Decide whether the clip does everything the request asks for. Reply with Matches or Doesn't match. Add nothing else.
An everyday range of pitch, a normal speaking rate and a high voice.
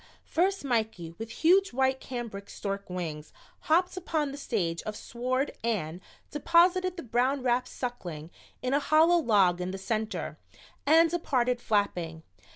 Doesn't match